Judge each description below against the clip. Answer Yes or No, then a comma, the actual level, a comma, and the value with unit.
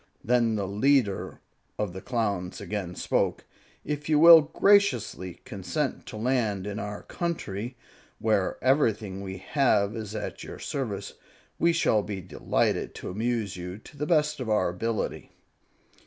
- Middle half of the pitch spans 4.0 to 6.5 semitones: Yes, average, 5.2 semitones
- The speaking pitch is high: No, low, 110 Hz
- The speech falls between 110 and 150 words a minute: Yes, average, 145 wpm